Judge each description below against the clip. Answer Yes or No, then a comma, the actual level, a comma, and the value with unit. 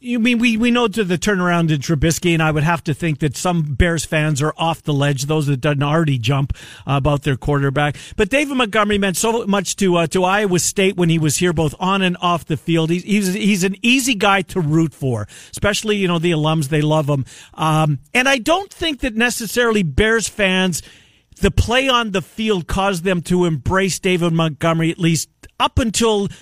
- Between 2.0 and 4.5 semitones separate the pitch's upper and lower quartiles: No, average, 4.9 semitones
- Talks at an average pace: No, fast, 215 wpm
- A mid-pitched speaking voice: Yes, medium, 175 Hz